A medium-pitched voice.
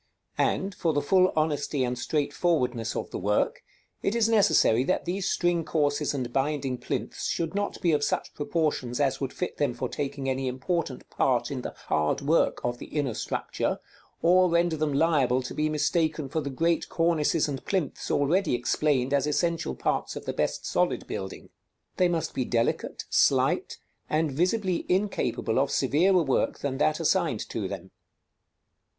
Yes: medium, 150 Hz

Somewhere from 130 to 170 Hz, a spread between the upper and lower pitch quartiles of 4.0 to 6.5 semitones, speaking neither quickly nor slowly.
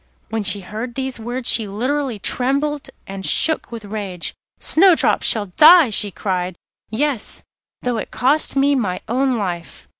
No: high, 235 Hz; average, 5.2 semitones; average, 150 wpm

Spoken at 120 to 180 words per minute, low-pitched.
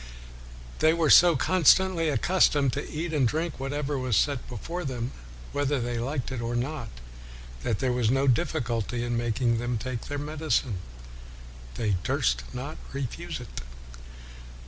Yes: average, 145 wpm; low, 130 Hz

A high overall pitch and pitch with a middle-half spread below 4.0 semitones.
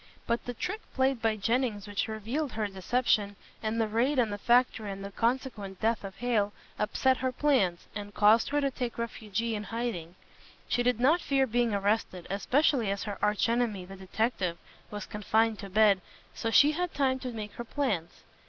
Yes: high, 225 Hz; average, 3.4 semitones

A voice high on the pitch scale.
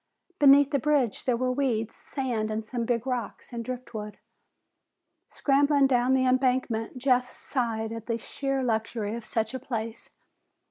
Yes: very high, 250 Hz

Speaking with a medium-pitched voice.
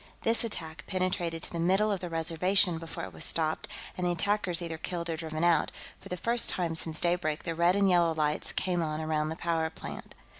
Yes: medium, 170 Hz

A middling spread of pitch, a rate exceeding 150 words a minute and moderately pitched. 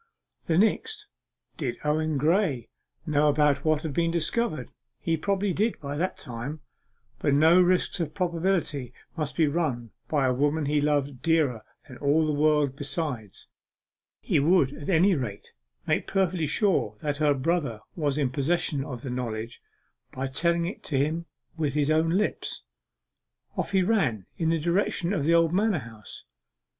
Yes: average, 3.5 semitones; average, 160 wpm; medium, 155 Hz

